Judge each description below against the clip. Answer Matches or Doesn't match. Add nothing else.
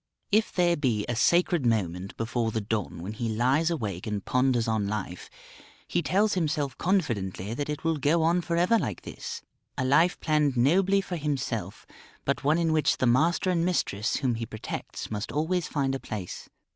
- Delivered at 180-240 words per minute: Matches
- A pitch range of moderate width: Doesn't match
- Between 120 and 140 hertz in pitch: Matches